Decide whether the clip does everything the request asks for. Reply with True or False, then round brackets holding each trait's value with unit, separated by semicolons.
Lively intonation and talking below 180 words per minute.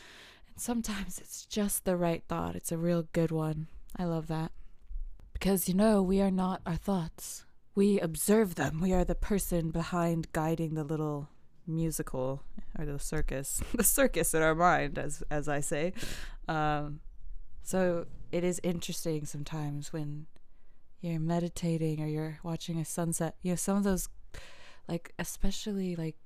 False (2.9 semitones; 155 wpm)